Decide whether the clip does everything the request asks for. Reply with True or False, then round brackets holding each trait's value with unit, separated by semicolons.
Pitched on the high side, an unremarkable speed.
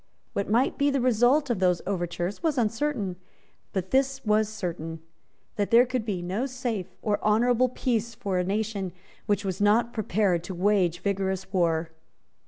True (210 Hz; 165 wpm)